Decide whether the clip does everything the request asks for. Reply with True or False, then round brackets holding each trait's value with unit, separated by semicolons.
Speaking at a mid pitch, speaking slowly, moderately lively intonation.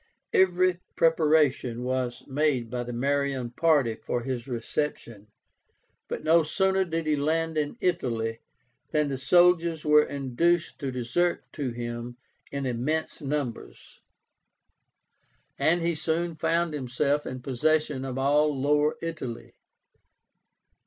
True (145 Hz; 120 wpm; 4.4 semitones)